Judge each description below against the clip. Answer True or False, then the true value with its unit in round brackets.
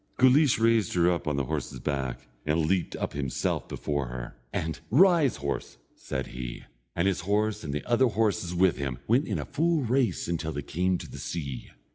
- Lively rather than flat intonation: True (8.2 semitones)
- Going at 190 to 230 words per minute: True (195 wpm)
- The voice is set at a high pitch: False (85 Hz)